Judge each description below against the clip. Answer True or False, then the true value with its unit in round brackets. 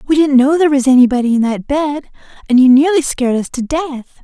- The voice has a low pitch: False (275 Hz)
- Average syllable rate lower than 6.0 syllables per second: False (6.6 syllables/s)